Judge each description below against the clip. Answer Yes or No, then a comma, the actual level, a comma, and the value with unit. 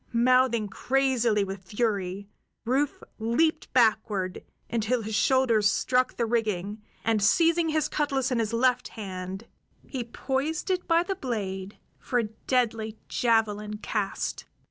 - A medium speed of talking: No, slow, 130 wpm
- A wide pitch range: No, average, 3.9 semitones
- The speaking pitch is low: No, high, 230 Hz